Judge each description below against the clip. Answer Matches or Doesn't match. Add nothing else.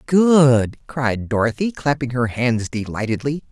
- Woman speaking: Doesn't match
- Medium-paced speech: Doesn't match